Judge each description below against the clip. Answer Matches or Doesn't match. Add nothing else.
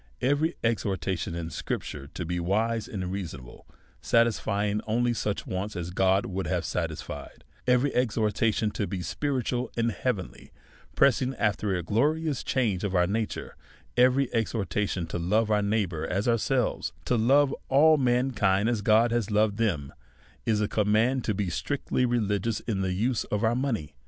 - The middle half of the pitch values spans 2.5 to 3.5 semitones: Doesn't match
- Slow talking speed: Doesn't match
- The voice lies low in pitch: Matches